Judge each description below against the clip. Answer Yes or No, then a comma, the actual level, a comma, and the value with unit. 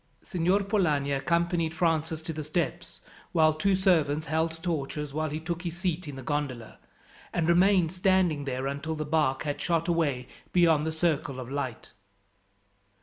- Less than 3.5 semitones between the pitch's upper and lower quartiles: Yes, average, 2.9 semitones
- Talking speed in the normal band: Yes, average, 160 wpm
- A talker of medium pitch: Yes, medium, 160 Hz